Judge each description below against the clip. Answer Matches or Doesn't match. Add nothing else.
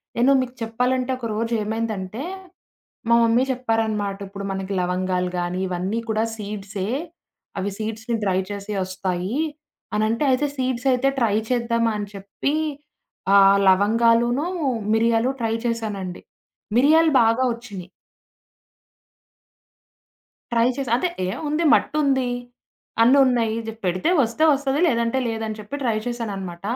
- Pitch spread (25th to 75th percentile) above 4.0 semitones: Doesn't match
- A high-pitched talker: Matches